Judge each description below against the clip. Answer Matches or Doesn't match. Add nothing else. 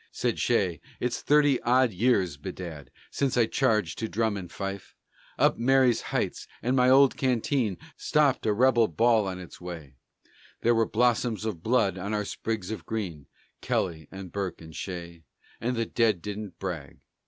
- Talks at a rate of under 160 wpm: Doesn't match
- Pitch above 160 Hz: Doesn't match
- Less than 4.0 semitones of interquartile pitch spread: Doesn't match